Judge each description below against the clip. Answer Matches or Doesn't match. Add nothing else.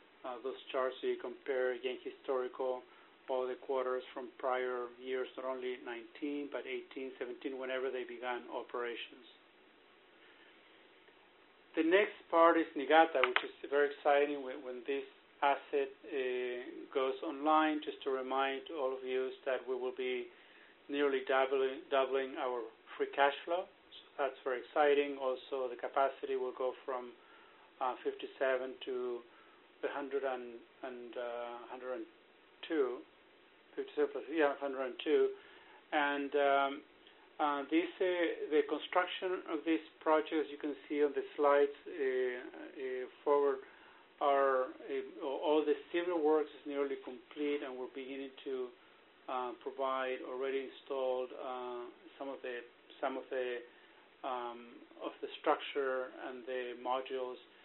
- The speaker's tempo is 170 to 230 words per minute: Doesn't match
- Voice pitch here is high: Doesn't match